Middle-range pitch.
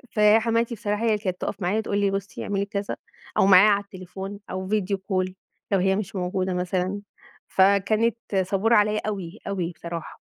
No: high, 200 Hz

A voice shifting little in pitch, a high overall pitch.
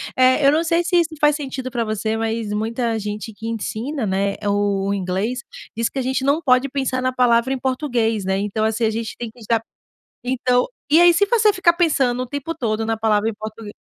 No: average, 3.9 semitones; high, 235 Hz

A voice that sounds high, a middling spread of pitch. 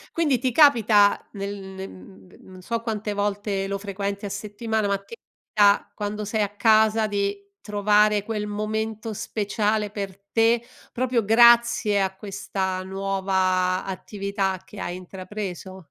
No: high, 205 Hz; narrow, 2.0 semitones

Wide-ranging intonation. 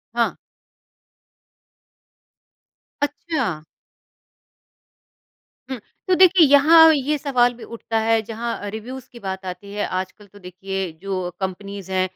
Yes: wide, 5.8 semitones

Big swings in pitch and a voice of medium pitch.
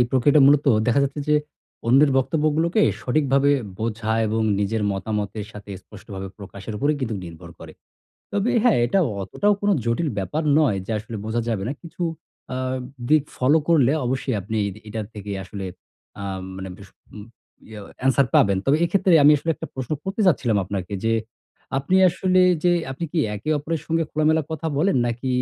No: wide, 6.5 semitones; low, 130 Hz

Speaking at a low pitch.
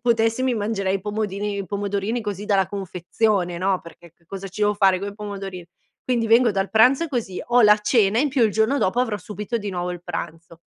No: high, 205 Hz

